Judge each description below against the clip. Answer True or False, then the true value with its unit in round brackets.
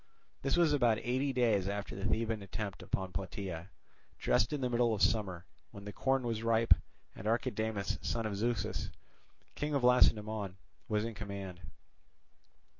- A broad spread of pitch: False (3.3 semitones)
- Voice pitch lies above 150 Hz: False (110 Hz)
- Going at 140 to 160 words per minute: True (155 wpm)